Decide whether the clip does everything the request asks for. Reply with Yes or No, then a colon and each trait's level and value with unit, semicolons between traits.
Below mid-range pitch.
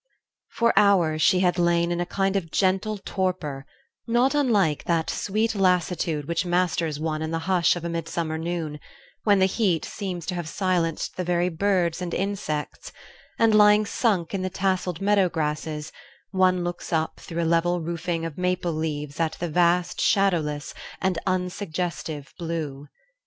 No: medium, 175 Hz